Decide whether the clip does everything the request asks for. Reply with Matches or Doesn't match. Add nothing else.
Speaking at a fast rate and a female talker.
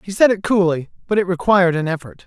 Doesn't match